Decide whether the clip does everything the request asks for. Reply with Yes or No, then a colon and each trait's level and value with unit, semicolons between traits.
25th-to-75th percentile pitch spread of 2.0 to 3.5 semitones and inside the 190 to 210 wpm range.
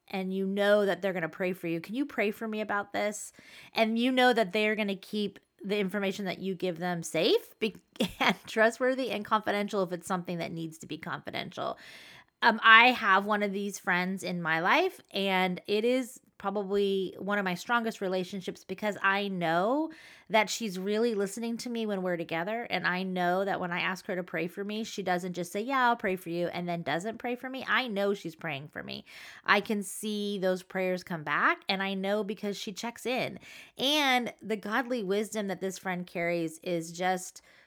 Yes: average, 3.2 semitones; fast, 205 wpm